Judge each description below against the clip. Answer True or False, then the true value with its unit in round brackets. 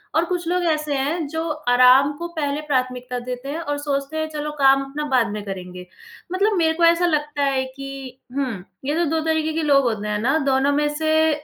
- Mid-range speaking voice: False (285 Hz)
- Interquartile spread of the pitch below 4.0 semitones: True (3.3 semitones)